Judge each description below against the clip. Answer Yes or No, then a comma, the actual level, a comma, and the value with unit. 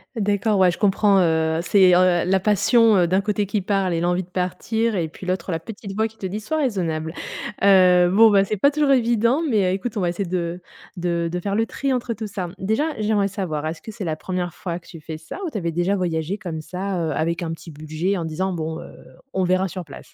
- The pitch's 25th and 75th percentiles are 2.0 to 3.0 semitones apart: No, average, 3.5 semitones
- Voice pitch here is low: No, medium, 185 Hz